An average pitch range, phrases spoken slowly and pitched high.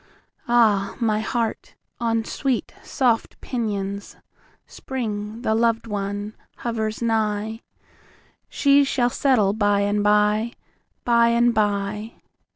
No: narrow, 2.2 semitones; slow, 90 wpm; high, 220 Hz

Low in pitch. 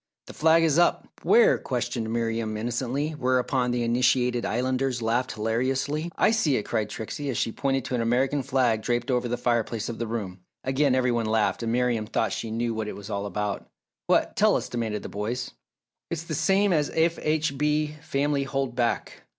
Yes: low, 125 Hz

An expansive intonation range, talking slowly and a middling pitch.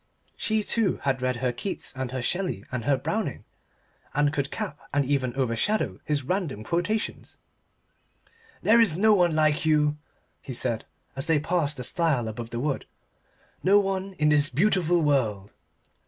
No: wide, 5.7 semitones; average, 160 wpm; medium, 145 Hz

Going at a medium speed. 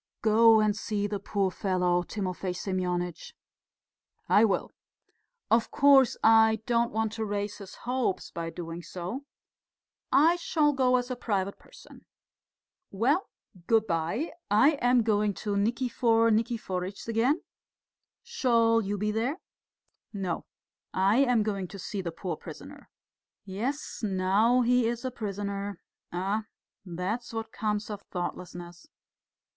No: slow, 130 wpm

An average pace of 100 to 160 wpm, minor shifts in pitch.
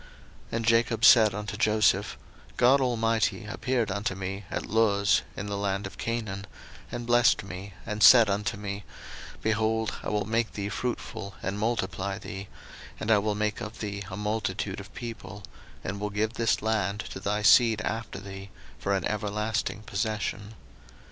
No: average, 170 wpm; narrow, 2.0 semitones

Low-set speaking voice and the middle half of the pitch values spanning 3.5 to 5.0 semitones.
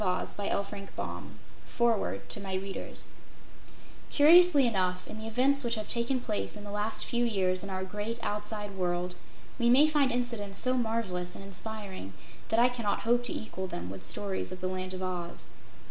No: high, 210 Hz; average, 4.1 semitones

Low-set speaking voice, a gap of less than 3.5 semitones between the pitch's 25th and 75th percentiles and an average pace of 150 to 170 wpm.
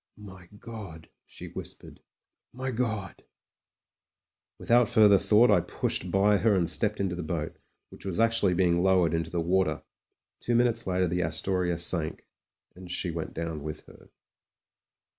No: very low, 95 Hz; average, 3.8 semitones; average, 160 wpm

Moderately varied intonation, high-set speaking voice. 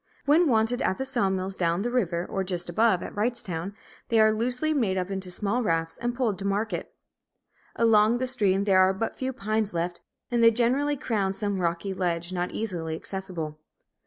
Yes: average, 4.2 semitones; high, 200 Hz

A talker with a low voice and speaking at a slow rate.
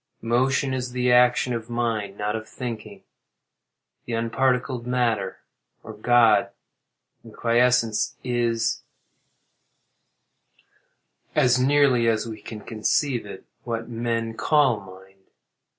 Yes: low, 115 Hz; slow, 105 wpm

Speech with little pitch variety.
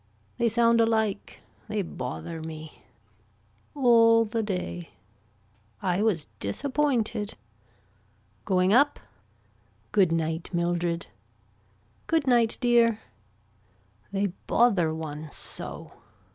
No: wide, 5.5 semitones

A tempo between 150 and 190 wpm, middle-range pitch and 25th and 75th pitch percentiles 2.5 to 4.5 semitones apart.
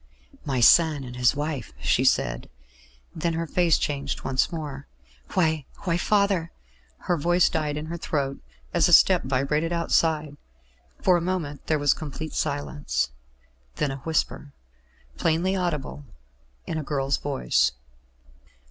No: average, 140 wpm; medium, 150 Hz; average, 3.2 semitones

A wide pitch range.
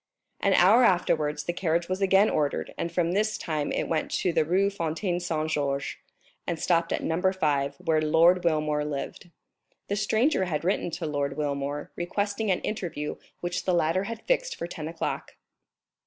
No: average, 3.6 semitones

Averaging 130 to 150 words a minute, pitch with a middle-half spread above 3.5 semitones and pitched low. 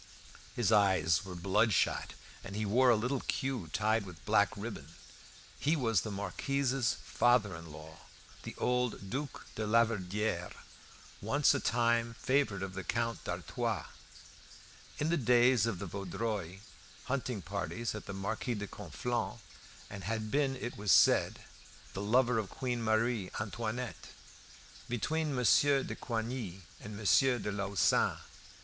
Yes: average, 140 wpm; average, 3.9 semitones; low, 110 Hz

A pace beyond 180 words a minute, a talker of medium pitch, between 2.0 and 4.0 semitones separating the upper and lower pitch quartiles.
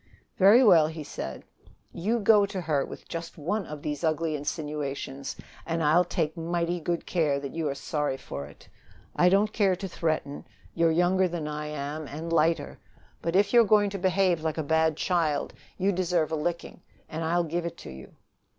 Yes: average, 195 wpm; medium, 165 Hz; average, 3.0 semitones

